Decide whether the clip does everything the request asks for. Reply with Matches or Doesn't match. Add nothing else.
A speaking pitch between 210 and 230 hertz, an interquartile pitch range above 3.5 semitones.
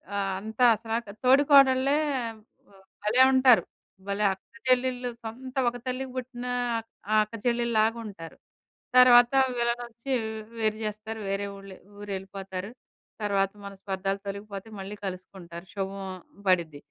Matches